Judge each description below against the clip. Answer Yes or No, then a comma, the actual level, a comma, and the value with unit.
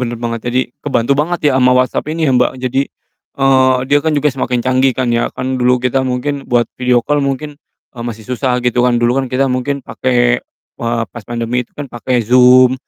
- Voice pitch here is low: Yes, low, 125 Hz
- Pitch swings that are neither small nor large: No, narrow, 1.7 semitones